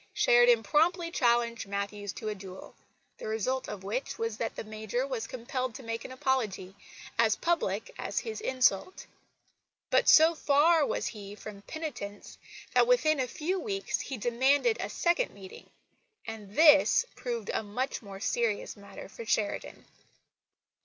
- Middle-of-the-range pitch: No, high, 240 Hz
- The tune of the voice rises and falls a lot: Yes, wide, 6.0 semitones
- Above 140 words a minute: Yes, average, 155 wpm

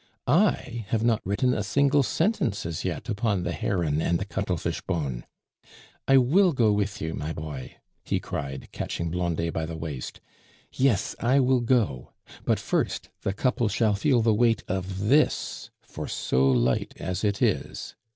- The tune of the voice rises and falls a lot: Yes, wide, 6.5 semitones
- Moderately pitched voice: No, low, 100 Hz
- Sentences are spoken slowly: No, average, 165 wpm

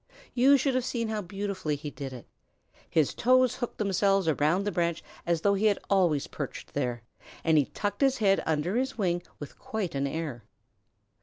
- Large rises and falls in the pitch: Yes, wide, 5.9 semitones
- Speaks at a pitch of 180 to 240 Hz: Yes, high, 190 Hz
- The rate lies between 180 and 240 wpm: Yes, average, 185 wpm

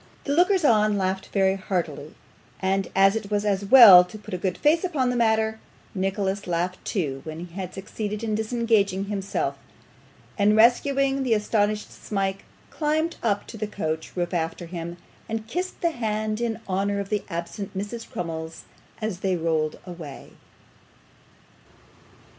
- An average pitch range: Yes, average, 3.3 semitones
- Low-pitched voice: No, high, 200 Hz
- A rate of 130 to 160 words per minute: Yes, average, 155 wpm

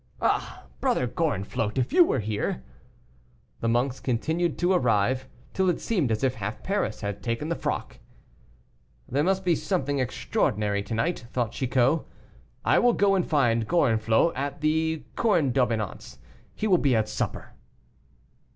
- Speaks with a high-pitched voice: No, low, 130 Hz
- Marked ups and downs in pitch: Yes, wide, 6.7 semitones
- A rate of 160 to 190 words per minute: No, average, 150 wpm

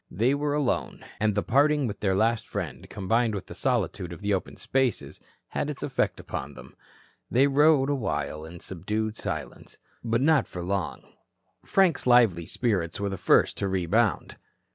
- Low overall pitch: Yes, low, 110 Hz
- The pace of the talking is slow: No, average, 165 wpm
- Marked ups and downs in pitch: Yes, wide, 5.8 semitones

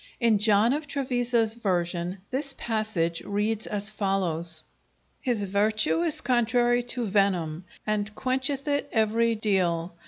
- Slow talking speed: Yes, slow, 125 wpm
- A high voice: Yes, high, 215 Hz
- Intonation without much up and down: No, average, 3.8 semitones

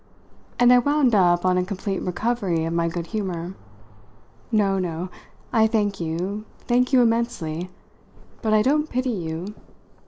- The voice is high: Yes, high, 200 Hz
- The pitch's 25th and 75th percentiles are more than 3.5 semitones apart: Yes, average, 5.1 semitones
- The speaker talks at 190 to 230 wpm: No, average, 150 wpm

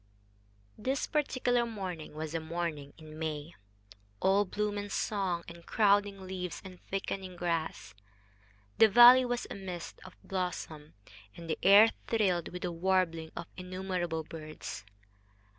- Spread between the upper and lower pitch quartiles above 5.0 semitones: No, average, 3.5 semitones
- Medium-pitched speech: Yes, medium, 180 Hz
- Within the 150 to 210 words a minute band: No, slow, 135 wpm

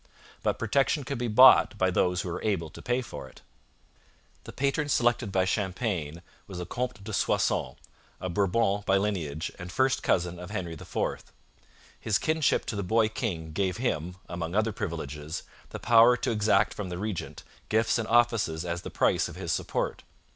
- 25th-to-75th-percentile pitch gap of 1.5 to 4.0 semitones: No, average, 4.9 semitones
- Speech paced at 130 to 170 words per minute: No, average, 180 wpm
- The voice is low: Yes, low, 100 Hz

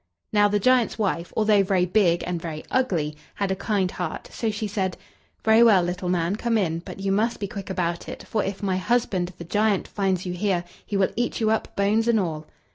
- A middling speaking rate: No, fast, 220 wpm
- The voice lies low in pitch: No, high, 195 Hz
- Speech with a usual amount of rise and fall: Yes, average, 3.2 semitones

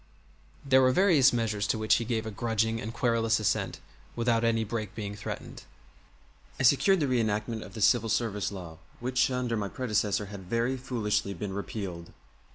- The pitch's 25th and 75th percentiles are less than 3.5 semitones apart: Yes, average, 2.8 semitones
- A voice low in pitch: Yes, low, 115 Hz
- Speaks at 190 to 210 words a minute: No, average, 170 wpm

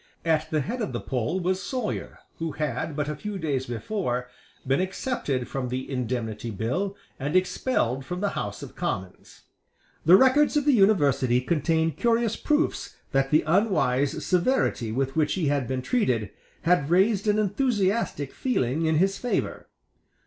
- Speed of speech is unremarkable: Yes, average, 160 wpm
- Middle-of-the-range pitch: Yes, medium, 160 Hz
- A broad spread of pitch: Yes, wide, 7.5 semitones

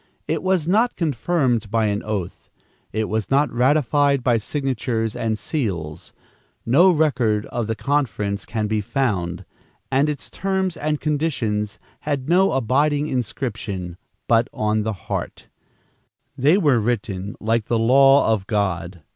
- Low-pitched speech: Yes, low, 120 Hz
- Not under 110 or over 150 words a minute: Yes, average, 140 wpm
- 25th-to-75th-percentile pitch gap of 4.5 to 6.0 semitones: Yes, wide, 5.5 semitones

